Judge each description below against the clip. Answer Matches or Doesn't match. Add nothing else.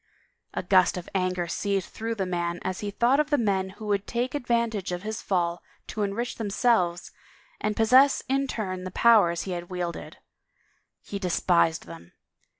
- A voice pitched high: Matches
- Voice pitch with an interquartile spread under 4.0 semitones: Doesn't match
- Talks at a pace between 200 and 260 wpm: Doesn't match